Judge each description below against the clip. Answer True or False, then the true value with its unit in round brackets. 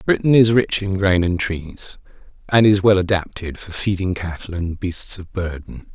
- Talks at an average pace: True (180 wpm)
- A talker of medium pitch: False (95 Hz)